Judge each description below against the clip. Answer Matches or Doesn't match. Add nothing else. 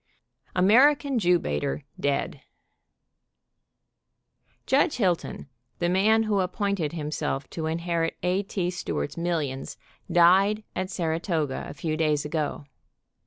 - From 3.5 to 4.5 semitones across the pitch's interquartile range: Matches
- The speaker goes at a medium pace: Doesn't match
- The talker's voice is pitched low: Doesn't match